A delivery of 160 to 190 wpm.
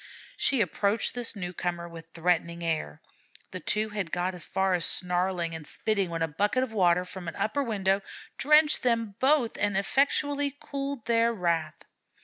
Yes: average, 165 wpm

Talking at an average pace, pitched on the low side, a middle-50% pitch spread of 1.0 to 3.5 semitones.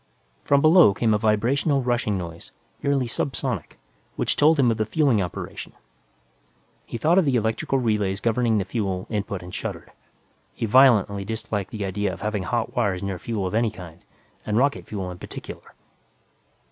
No: average, 170 wpm; low, 110 Hz; average, 4.1 semitones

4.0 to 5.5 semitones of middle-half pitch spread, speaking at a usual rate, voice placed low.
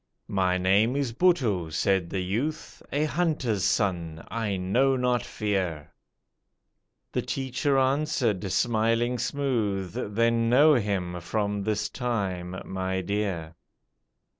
No: average, 5.1 semitones; slow, 115 wpm; low, 105 Hz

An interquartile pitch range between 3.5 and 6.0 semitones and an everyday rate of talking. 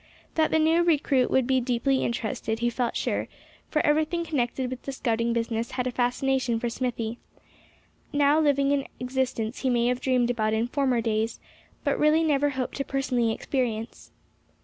No: average, 3.1 semitones; average, 170 wpm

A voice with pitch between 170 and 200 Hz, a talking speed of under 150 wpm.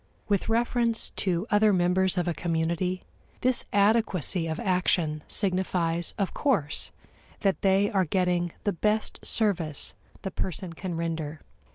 Yes: medium, 185 Hz; slow, 135 wpm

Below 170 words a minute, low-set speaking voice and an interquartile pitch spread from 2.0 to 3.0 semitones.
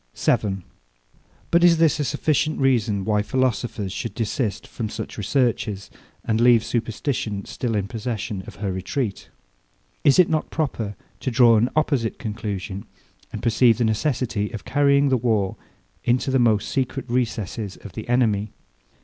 No: average, 150 wpm; low, 115 Hz; average, 3.9 semitones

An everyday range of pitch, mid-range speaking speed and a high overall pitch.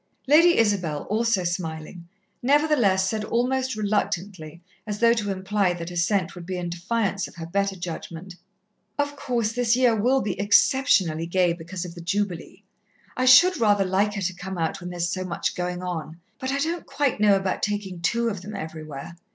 Yes: average, 4.8 semitones; average, 185 wpm; high, 195 Hz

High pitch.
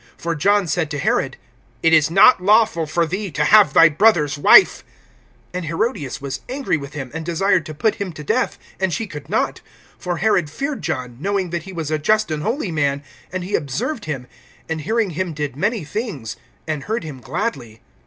No: medium, 165 Hz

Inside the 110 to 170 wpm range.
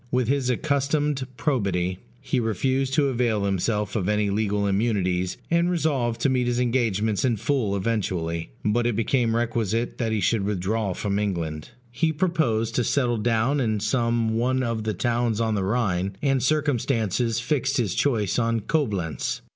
Yes: average, 165 wpm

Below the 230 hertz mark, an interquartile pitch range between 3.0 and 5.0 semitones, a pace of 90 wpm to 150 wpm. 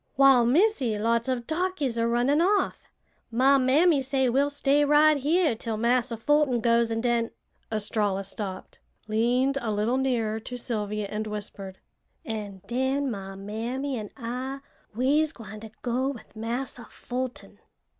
No: high, 240 Hz; average, 3.7 semitones; average, 145 wpm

